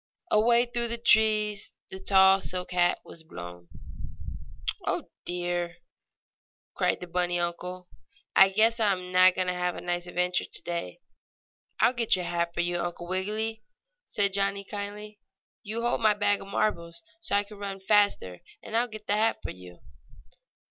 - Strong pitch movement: No, average, 3.2 semitones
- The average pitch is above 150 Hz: Yes, high, 190 Hz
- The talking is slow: No, average, 165 wpm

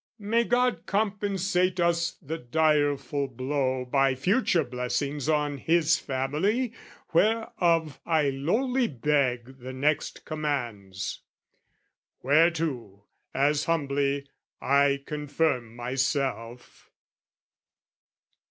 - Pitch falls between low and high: Yes, medium, 145 Hz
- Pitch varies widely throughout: No, average, 4.2 semitones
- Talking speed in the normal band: No, slow, 90 wpm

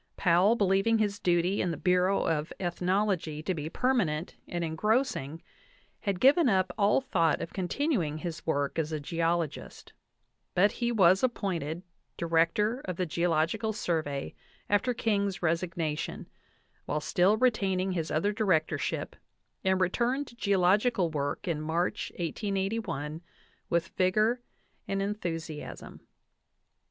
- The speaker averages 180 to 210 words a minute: No, slow, 135 wpm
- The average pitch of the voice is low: No, medium, 185 Hz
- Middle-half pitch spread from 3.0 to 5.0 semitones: Yes, average, 4.1 semitones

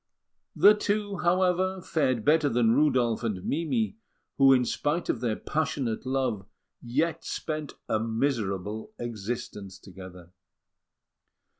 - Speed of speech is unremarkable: No, slow, 115 wpm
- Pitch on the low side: Yes, low, 130 Hz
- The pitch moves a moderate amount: No, wide, 6.3 semitones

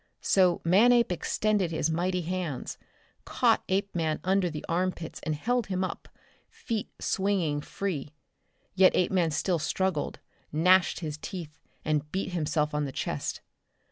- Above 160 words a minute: No, slow, 135 wpm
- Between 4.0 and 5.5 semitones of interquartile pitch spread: No, average, 3.5 semitones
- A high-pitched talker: No, medium, 180 Hz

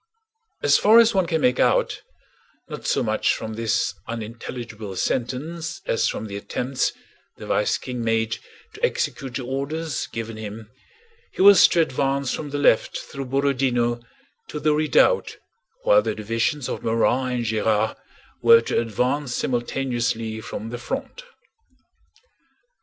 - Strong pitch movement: No, average, 4.6 semitones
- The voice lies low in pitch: Yes, low, 125 Hz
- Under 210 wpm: Yes, average, 140 wpm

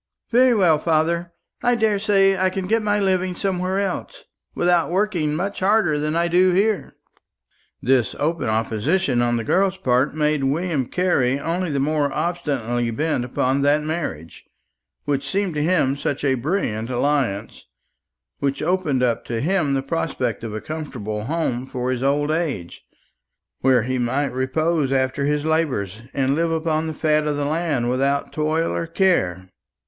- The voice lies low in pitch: No, medium, 150 Hz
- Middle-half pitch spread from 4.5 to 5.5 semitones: Yes, average, 5.0 semitones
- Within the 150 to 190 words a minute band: Yes, average, 160 wpm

